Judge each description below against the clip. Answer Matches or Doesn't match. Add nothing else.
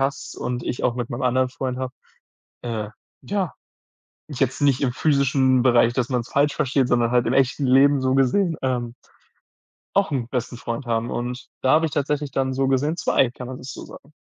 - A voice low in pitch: Matches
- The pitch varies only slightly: Matches